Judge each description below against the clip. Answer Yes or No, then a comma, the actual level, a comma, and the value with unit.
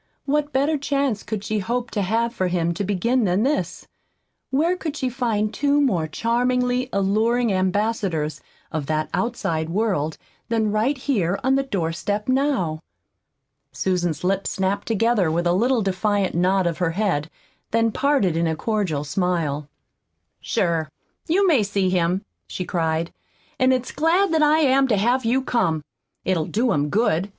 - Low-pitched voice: No, high, 210 Hz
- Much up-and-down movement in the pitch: Yes, wide, 6.3 semitones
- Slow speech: No, average, 160 wpm